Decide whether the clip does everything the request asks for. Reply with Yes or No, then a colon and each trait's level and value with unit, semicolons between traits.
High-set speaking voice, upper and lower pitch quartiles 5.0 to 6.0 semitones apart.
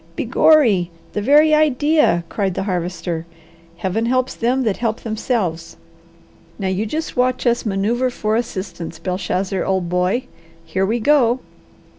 Yes: high, 215 Hz; wide, 5.4 semitones